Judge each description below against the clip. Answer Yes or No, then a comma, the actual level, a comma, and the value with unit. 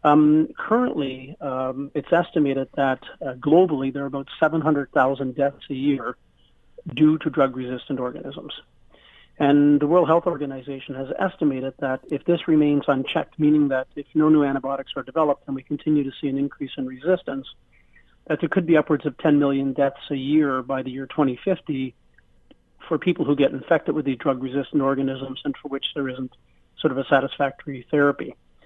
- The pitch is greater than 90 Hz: Yes, medium, 140 Hz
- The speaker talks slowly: No, average, 175 wpm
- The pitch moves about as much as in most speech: No, narrow, 2.3 semitones